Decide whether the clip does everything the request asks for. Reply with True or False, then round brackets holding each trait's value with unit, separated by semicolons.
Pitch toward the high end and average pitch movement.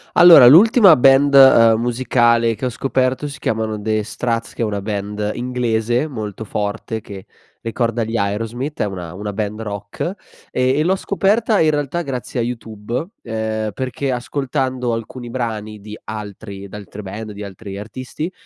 False (115 Hz; 3.6 semitones)